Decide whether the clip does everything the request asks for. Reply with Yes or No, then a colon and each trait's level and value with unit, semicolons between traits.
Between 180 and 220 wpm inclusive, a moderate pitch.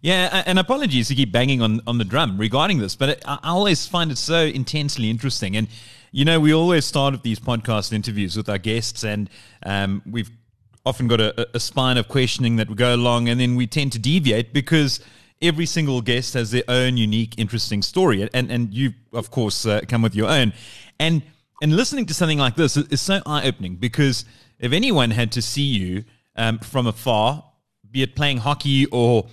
No: fast, 205 wpm; low, 125 Hz